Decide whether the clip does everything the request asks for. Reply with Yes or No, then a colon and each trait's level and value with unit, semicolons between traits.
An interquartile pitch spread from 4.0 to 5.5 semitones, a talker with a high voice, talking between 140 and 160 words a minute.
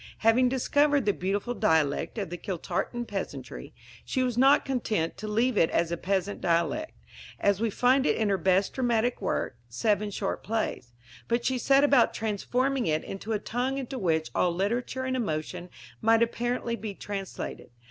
No: average, 4.6 semitones; high, 220 Hz; average, 170 wpm